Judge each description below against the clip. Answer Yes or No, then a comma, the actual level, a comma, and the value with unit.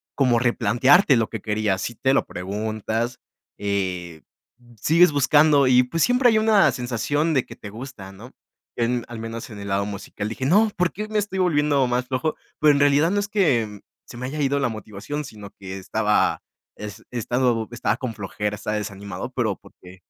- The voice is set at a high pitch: No, low, 120 Hz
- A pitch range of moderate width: No, wide, 5.7 semitones